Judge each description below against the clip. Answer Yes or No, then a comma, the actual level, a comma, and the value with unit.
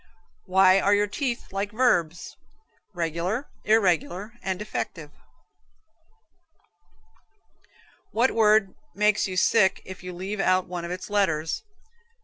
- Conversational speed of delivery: No, slow, 115 wpm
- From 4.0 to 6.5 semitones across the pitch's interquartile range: No, average, 2.8 semitones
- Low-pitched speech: No, high, 190 Hz